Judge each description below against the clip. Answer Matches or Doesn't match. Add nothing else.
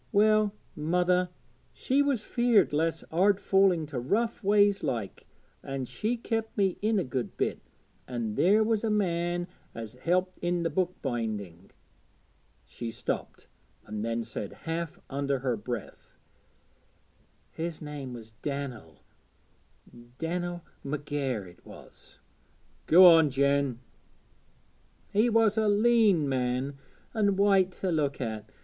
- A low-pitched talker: Doesn't match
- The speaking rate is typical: Doesn't match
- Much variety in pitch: Matches